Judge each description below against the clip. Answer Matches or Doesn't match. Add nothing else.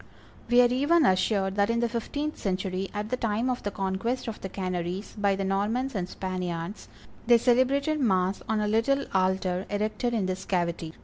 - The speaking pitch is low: Doesn't match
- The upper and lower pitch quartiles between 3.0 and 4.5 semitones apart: Matches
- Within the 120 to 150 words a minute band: Doesn't match